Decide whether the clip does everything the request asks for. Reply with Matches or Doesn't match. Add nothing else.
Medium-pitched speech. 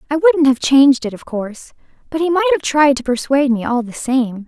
Doesn't match